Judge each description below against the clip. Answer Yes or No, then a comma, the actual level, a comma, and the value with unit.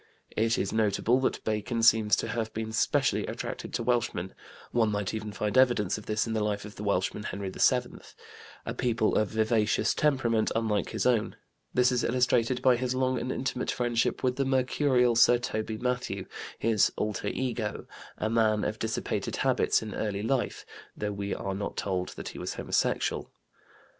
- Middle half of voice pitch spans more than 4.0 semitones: No, average, 2.7 semitones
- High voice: No, low, 110 Hz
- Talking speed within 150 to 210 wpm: Yes, average, 180 wpm